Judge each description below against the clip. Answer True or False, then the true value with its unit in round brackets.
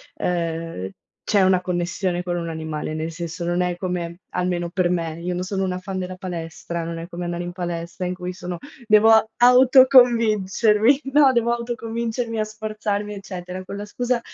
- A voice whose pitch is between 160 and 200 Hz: True (185 Hz)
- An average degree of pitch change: True (3.8 semitones)